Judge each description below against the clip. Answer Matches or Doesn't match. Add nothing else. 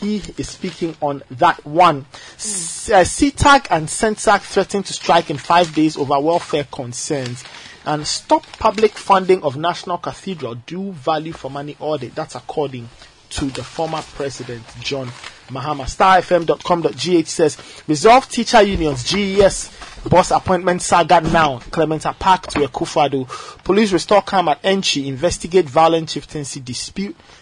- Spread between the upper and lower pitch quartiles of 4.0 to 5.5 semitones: Matches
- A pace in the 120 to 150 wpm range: Matches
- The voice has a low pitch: Doesn't match